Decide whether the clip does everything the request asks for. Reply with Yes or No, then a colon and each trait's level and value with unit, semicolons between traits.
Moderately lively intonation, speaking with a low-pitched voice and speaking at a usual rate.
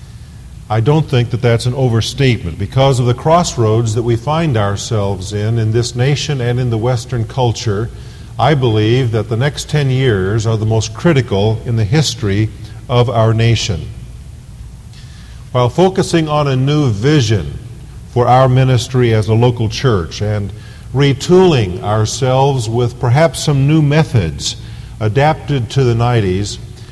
Yes: average, 3.4 semitones; low, 120 Hz; average, 145 wpm